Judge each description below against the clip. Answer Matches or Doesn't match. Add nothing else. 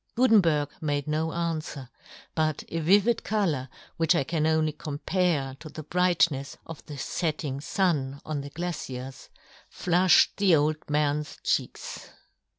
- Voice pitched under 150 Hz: Doesn't match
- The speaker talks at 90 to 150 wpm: Matches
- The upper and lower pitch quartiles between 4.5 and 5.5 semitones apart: Doesn't match